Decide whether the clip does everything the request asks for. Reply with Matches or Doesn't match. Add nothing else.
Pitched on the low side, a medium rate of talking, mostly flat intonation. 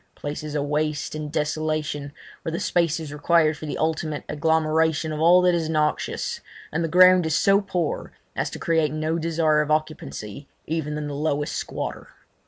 Doesn't match